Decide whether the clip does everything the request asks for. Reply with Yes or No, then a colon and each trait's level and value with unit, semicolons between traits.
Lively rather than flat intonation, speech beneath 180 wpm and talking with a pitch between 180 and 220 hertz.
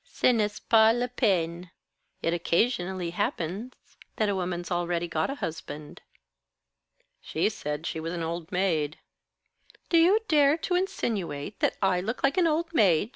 Yes: wide, 6.4 semitones; average, 155 wpm; medium, 185 Hz